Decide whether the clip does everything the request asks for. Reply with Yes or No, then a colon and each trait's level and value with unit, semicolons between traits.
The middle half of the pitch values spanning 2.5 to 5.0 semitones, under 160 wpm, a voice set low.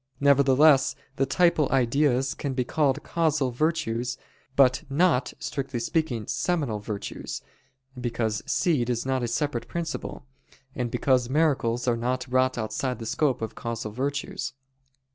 Yes: average, 3.2 semitones; slow, 135 wpm; low, 130 Hz